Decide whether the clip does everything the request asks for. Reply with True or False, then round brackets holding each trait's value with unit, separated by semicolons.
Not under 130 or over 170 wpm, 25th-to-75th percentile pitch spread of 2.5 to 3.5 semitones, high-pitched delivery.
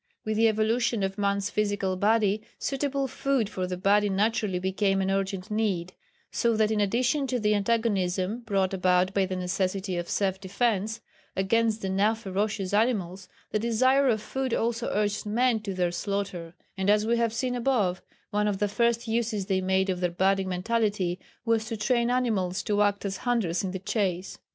False (185 wpm; 3.2 semitones; 205 Hz)